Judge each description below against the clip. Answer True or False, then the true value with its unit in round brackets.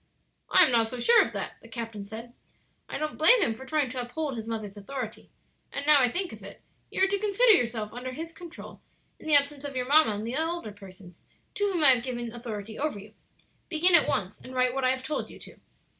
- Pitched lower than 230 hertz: False (255 Hz)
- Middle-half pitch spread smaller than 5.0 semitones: False (5.6 semitones)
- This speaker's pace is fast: True (240 wpm)